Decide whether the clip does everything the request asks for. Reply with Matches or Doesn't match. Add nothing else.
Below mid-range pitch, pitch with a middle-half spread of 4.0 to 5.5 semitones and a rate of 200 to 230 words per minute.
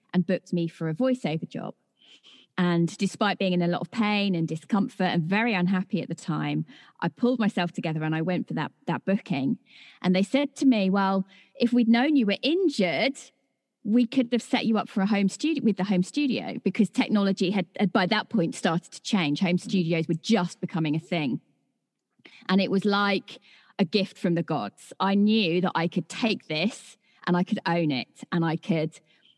Doesn't match